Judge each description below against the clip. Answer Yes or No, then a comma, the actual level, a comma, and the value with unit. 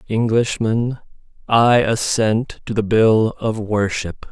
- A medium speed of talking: No, slow, 110 wpm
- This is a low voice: Yes, low, 110 Hz